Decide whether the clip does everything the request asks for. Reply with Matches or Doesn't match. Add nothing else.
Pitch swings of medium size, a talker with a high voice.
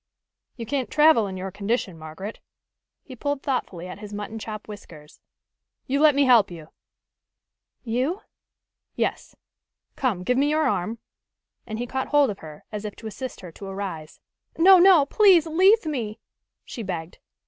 Doesn't match